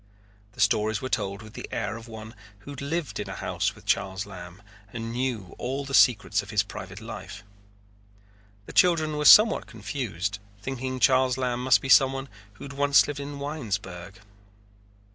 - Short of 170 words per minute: No, average, 175 wpm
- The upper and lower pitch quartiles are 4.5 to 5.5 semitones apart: Yes, average, 5.0 semitones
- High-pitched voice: No, low, 120 Hz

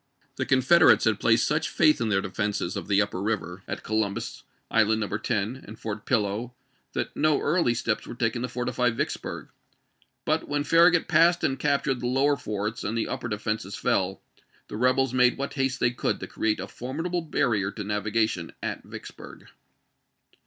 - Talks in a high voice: No, low, 115 Hz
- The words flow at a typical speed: Yes, average, 180 wpm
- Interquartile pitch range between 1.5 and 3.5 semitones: No, average, 4.2 semitones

